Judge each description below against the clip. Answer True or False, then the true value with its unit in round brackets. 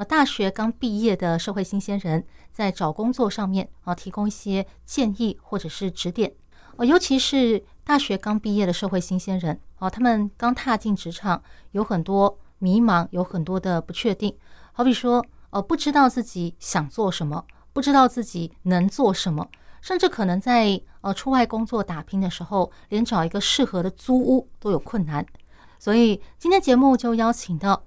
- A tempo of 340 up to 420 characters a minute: False (265 characters per minute)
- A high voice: True (205 Hz)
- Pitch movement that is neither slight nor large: True (4.5 semitones)